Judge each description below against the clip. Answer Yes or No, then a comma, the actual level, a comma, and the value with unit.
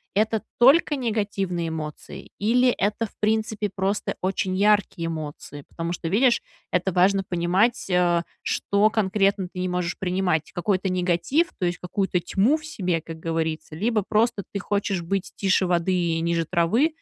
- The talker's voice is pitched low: No, high, 190 Hz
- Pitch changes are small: No, average, 3.5 semitones